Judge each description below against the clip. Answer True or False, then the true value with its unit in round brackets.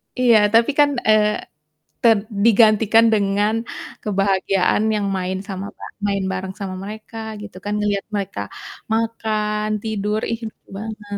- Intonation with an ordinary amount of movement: False (1.9 semitones)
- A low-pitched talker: False (210 Hz)